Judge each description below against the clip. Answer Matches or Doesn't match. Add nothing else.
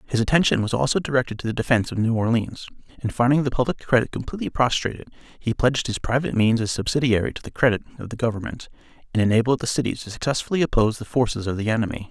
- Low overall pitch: Matches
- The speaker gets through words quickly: Matches